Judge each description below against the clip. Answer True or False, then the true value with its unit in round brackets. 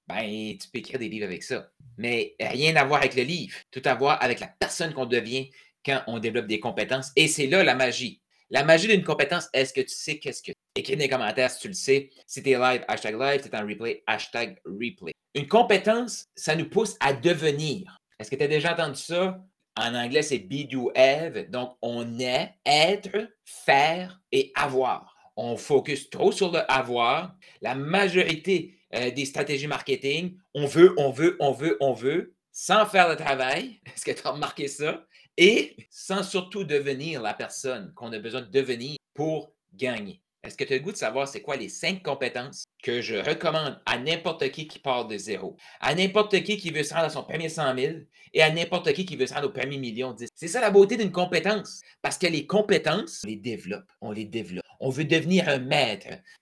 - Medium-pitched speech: True (150 Hz)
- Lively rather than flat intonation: True (6.2 semitones)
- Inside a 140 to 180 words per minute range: False (210 wpm)